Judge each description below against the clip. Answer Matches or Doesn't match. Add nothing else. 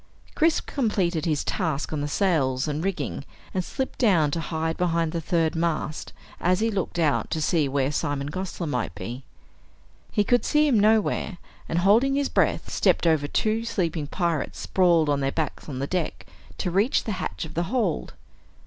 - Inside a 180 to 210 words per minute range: Matches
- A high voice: Doesn't match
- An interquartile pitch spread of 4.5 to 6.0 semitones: Matches